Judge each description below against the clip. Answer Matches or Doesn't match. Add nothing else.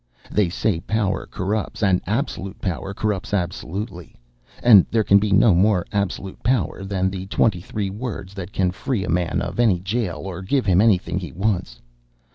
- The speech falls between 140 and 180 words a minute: Matches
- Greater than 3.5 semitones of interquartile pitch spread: Doesn't match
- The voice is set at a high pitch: Doesn't match